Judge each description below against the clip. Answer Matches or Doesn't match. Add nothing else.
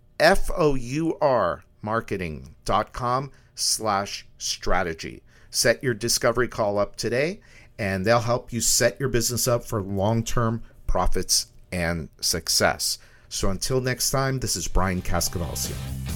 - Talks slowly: Matches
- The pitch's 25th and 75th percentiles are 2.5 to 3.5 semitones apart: Doesn't match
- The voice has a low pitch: Matches